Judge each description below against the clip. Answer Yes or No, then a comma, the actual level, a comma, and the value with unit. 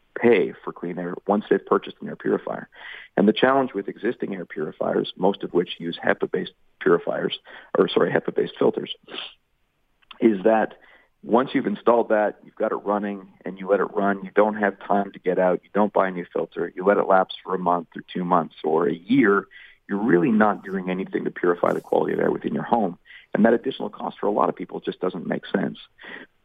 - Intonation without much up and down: Yes, narrow, 2.2 semitones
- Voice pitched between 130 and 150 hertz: No, low, 100 Hz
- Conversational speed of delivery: No, fast, 215 wpm